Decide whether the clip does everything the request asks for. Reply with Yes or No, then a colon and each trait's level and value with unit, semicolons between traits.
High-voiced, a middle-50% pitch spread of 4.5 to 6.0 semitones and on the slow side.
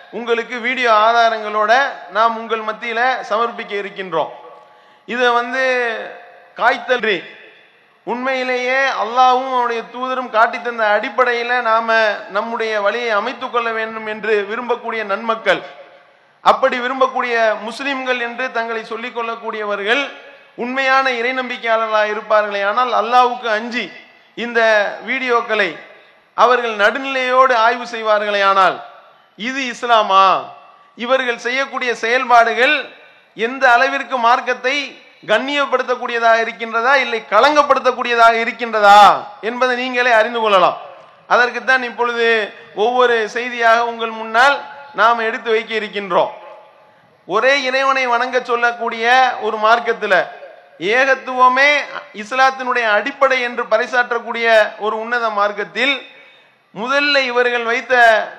No: high, 235 Hz; narrow, 2.4 semitones; slow, 95 wpm